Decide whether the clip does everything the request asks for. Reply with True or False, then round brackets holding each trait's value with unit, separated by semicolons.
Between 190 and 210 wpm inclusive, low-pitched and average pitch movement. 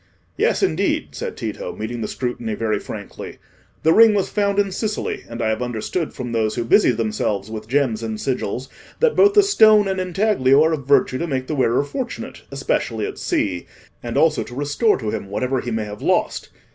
False (200 wpm; 130 Hz; 8.6 semitones)